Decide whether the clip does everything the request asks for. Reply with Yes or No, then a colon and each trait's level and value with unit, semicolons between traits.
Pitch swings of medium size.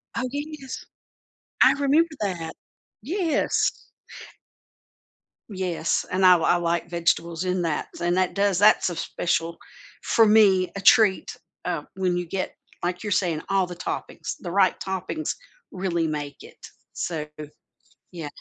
Yes: average, 3.0 semitones